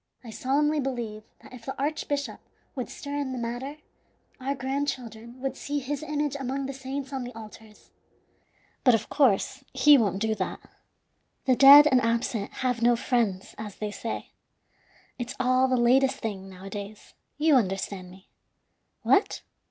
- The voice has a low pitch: No, very high, 255 Hz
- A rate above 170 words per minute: No, average, 155 wpm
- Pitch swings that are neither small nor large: Yes, average, 3.8 semitones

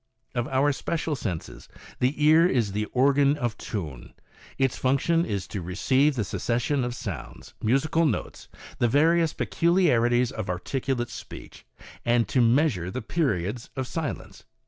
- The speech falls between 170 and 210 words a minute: No, average, 145 wpm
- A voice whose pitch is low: Yes, low, 125 Hz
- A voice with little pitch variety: No, average, 5.0 semitones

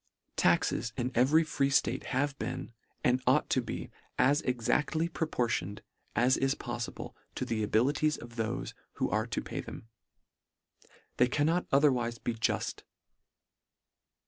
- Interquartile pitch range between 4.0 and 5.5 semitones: No, average, 3.6 semitones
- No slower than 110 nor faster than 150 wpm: Yes, slow, 135 wpm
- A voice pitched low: Yes, low, 130 Hz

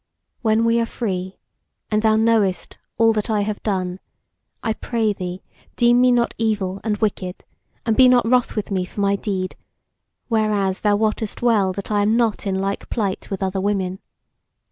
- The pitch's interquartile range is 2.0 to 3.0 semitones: Yes, average, 2.7 semitones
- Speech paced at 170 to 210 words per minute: Yes, average, 180 wpm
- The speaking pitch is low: No, high, 210 Hz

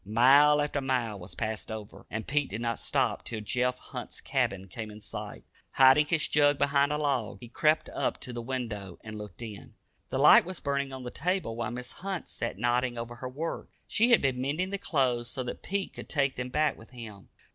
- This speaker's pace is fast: Yes, fast, 215 wpm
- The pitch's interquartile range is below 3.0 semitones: No, average, 4.2 semitones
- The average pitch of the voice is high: No, low, 125 Hz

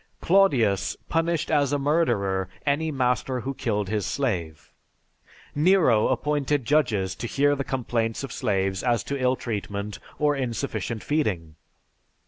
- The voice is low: Yes, low, 125 Hz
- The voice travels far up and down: Yes, wide, 5.7 semitones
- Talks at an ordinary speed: No, slow, 130 wpm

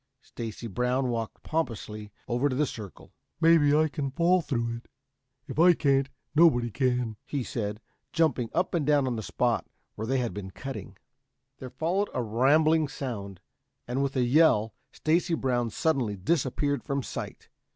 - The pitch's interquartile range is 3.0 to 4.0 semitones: No, average, 4.8 semitones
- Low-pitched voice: Yes, low, 130 Hz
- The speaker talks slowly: No, average, 160 wpm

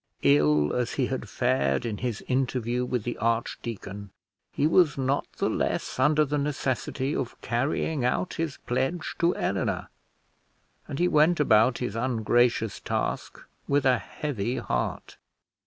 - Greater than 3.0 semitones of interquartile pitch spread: Yes, average, 3.6 semitones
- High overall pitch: No, low, 125 Hz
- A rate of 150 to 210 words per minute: No, average, 140 wpm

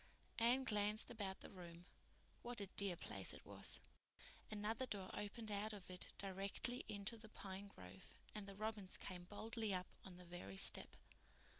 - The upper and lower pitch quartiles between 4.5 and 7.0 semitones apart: No, average, 2.7 semitones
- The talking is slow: No, average, 165 wpm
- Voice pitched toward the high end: Yes, high, 200 Hz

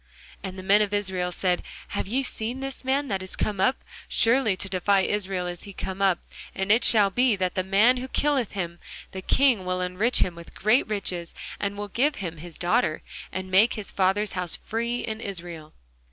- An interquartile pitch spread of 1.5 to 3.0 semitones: No, average, 3.5 semitones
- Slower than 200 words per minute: No, fast, 205 wpm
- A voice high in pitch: Yes, high, 195 Hz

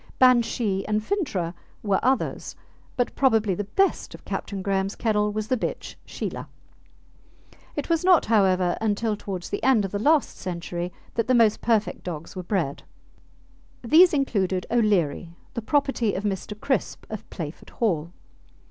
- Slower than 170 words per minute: Yes, average, 150 wpm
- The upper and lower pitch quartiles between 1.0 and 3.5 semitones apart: No, average, 4.2 semitones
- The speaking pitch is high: Yes, high, 210 Hz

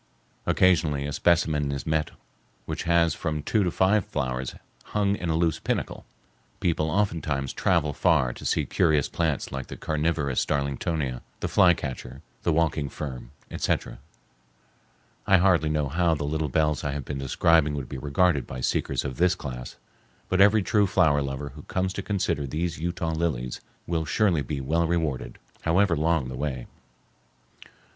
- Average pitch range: Yes, average, 3.4 semitones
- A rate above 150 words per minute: Yes, average, 165 wpm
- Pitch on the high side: No, very low, 75 Hz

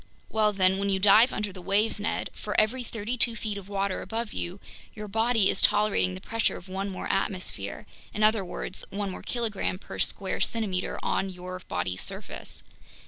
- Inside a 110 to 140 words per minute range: No, average, 195 wpm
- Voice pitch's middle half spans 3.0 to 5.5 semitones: No, narrow, 2.6 semitones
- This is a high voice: Yes, high, 200 Hz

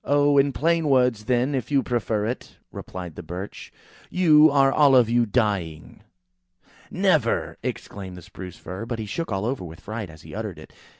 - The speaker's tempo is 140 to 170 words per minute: No, average, 185 wpm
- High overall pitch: No, low, 115 Hz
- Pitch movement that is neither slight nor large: No, wide, 6.2 semitones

